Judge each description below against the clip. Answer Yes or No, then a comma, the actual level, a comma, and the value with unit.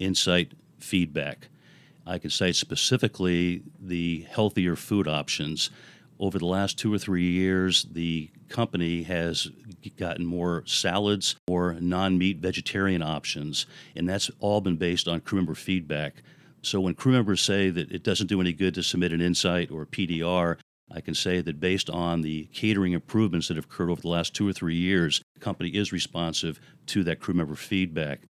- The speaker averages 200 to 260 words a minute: No, average, 175 wpm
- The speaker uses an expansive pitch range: No, narrow, 2.4 semitones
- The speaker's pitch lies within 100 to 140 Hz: No, very low, 90 Hz